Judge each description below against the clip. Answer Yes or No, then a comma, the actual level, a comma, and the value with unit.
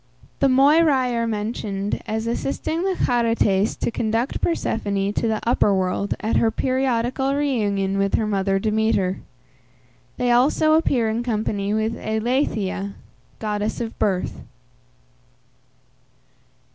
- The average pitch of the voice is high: Yes, high, 225 Hz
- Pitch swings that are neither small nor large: Yes, average, 3.6 semitones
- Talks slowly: Yes, slow, 120 wpm